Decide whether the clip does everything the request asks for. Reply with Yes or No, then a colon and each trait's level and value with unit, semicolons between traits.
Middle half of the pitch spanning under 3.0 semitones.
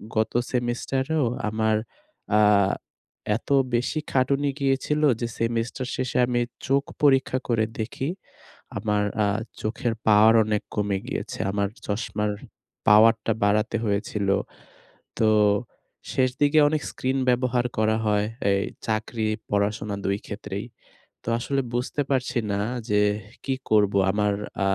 No: average, 3.7 semitones